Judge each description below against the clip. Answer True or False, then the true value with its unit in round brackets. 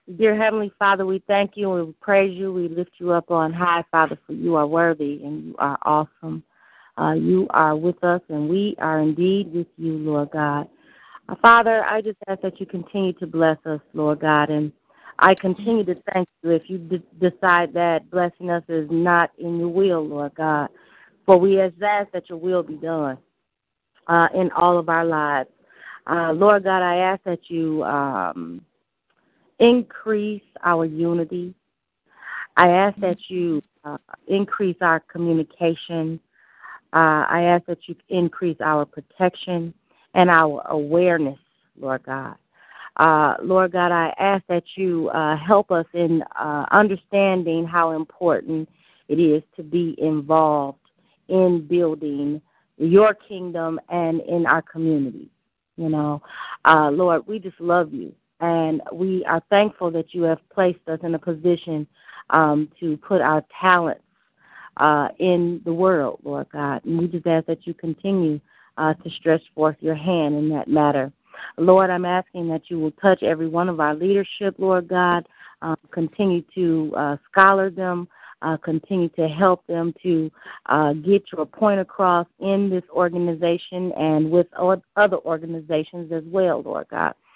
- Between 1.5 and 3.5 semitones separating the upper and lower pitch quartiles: True (2.7 semitones)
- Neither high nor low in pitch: True (170 Hz)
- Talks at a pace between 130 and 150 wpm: False (160 wpm)